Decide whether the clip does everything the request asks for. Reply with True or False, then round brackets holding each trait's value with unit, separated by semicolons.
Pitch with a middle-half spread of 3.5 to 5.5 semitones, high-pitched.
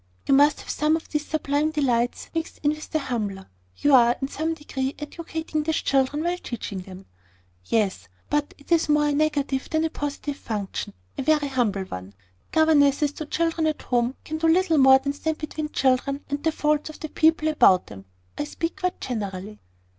True (3.8 semitones; 290 Hz)